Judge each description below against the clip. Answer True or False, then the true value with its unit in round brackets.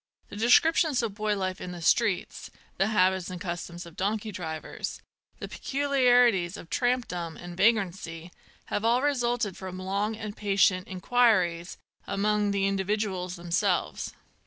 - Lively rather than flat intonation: False (3.8 semitones)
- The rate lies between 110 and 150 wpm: True (140 wpm)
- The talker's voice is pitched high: True (195 Hz)